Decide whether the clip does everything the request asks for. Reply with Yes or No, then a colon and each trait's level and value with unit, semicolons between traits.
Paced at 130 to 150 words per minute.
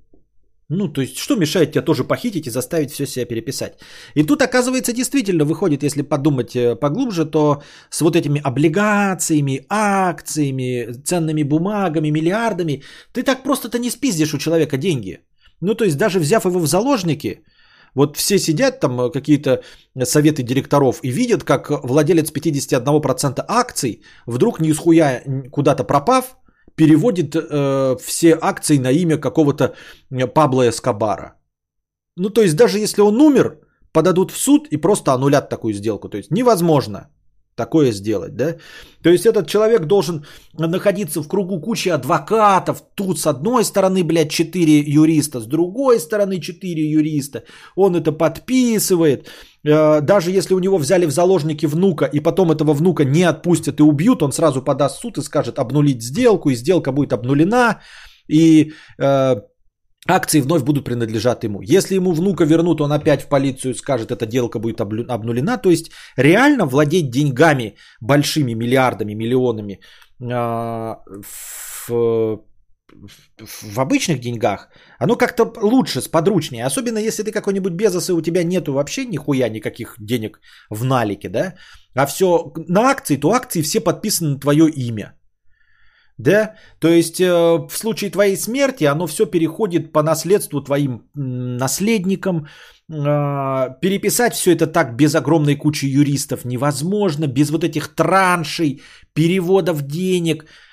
Yes: average, 145 wpm